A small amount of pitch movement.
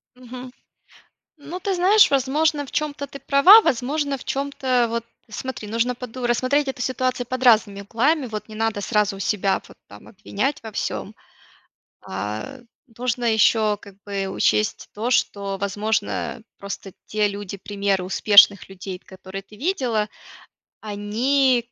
No: average, 4.6 semitones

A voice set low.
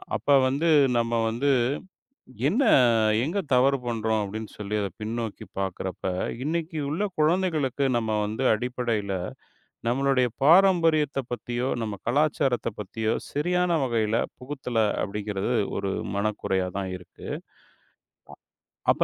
Yes: low, 120 Hz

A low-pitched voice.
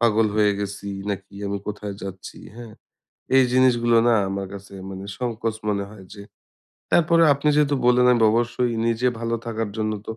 Yes: low, 115 Hz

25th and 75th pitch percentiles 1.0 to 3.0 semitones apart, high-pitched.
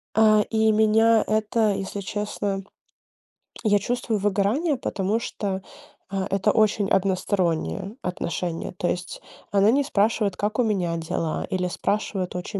Yes: narrow, 2.4 semitones; high, 205 Hz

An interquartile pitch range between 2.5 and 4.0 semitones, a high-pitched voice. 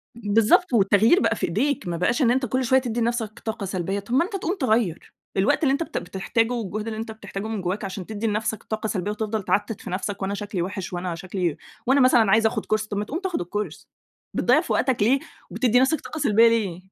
Yes: average, 3.5 semitones; high, 220 Hz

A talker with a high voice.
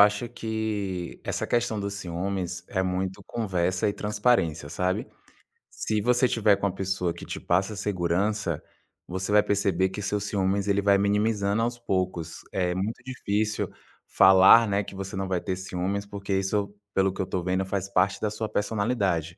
No: low, 100 Hz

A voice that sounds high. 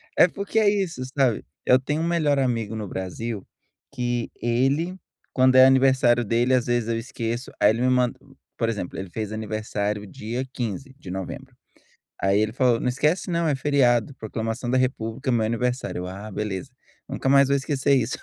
No: low, 120 Hz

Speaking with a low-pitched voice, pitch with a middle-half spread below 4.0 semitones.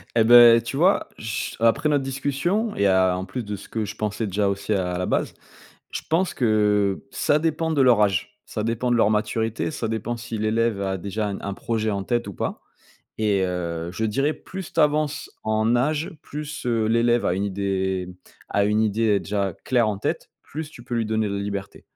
Yes: low, 110 Hz; average, 3.5 semitones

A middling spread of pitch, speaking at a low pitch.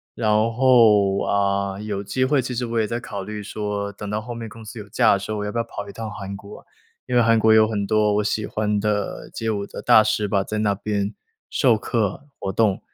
No: narrow, 1.8 semitones; low, 105 Hz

